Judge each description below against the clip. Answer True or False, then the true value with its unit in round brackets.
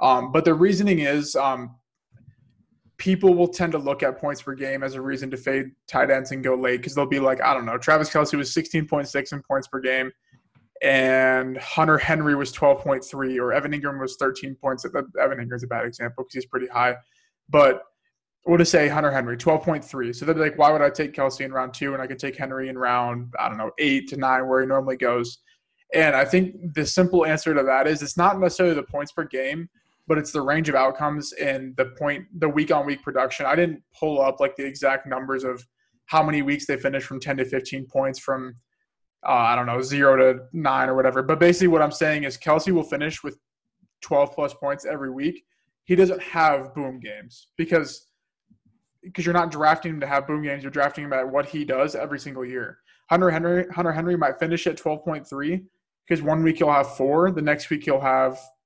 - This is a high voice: False (140 Hz)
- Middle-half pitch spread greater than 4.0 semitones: False (3.4 semitones)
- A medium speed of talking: False (220 wpm)